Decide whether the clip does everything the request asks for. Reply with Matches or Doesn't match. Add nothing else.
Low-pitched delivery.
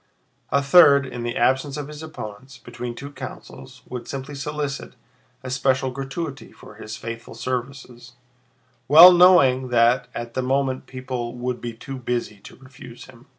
Matches